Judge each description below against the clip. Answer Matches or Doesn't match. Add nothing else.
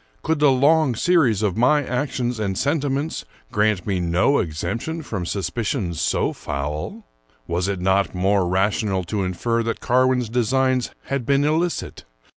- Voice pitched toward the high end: Doesn't match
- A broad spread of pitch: Matches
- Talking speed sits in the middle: Matches